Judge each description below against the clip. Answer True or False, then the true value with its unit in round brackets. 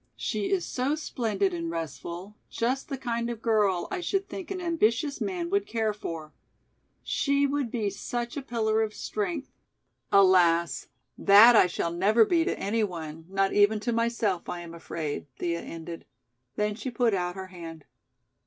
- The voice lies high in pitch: True (215 Hz)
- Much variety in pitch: True (5.8 semitones)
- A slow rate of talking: False (170 wpm)